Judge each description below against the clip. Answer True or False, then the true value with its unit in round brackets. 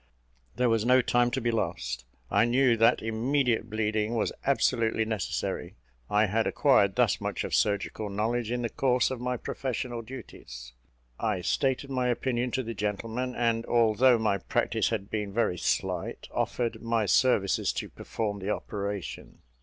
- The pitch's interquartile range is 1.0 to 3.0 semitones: True (2.7 semitones)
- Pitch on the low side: True (115 Hz)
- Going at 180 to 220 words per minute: False (160 wpm)